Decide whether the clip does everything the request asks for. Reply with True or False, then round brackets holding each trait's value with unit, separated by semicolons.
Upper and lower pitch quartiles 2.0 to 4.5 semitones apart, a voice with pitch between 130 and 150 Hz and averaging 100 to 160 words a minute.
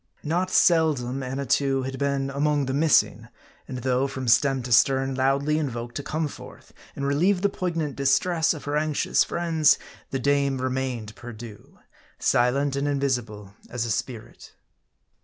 True (2.6 semitones; 135 Hz; 150 wpm)